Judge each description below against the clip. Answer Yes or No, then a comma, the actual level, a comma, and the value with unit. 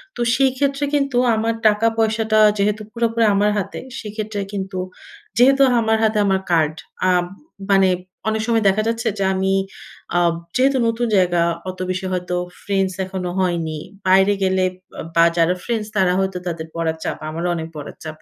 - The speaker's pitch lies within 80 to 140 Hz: No, high, 195 Hz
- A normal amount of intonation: Yes, average, 3.8 semitones